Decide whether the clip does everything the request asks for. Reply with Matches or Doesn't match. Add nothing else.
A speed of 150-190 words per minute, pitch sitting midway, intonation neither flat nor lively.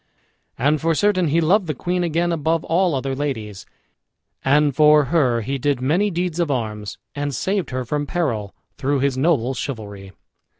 Matches